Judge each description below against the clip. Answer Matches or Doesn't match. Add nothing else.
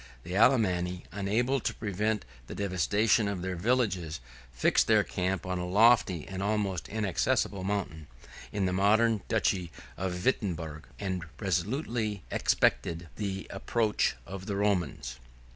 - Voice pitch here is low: Matches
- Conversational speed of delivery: Doesn't match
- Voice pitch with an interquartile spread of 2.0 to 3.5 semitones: Matches